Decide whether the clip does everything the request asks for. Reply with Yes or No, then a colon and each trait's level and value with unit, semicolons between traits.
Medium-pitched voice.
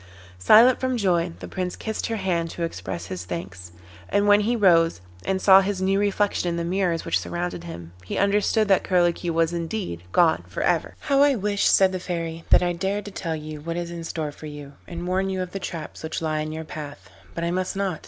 Yes: medium, 175 Hz